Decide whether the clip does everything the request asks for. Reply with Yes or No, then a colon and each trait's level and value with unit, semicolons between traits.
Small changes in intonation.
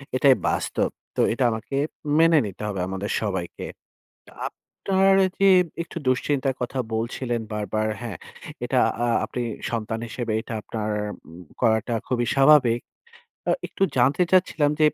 No: average, 4.3 semitones